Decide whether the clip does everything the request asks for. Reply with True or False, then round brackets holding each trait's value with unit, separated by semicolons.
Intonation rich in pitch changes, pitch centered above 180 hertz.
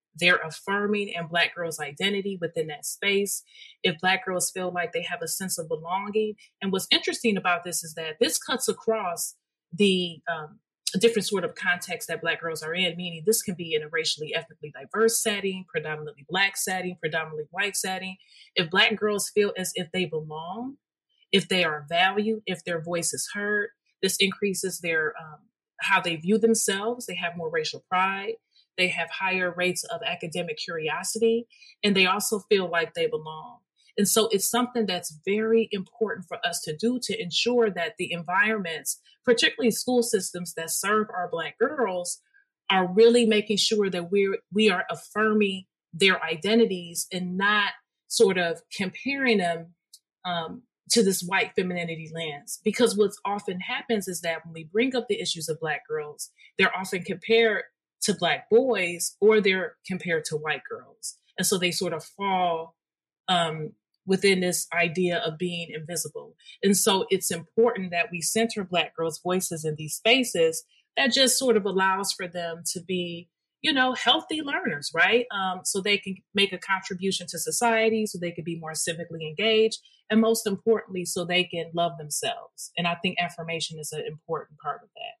False (4.6 semitones; 190 Hz)